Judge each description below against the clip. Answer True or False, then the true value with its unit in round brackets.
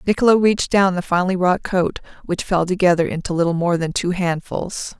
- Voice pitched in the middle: True (180 Hz)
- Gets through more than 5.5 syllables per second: True (5.7 syllables/s)